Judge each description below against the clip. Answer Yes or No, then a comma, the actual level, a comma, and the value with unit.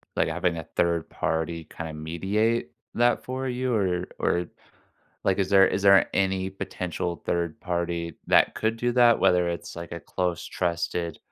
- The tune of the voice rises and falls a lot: No, average, 2.8 semitones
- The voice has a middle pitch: No, very low, 90 Hz